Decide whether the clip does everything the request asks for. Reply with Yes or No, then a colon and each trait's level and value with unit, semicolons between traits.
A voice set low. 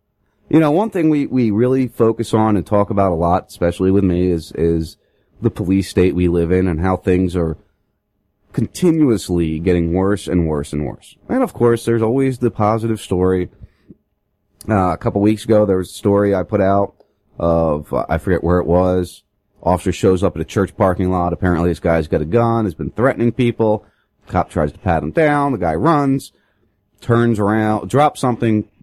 Yes: low, 100 Hz